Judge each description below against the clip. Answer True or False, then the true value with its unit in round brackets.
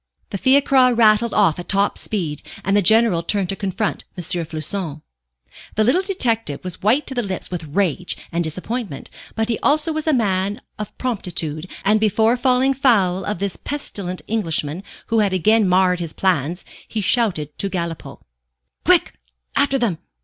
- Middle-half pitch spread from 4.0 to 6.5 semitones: True (4.6 semitones)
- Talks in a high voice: True (200 Hz)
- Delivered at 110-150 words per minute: False (165 wpm)